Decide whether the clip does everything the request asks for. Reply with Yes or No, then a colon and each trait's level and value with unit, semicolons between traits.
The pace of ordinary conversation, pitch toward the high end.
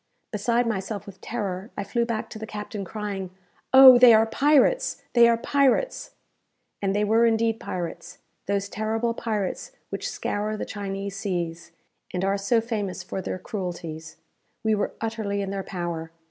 Yes: average, 160 wpm; high, 210 Hz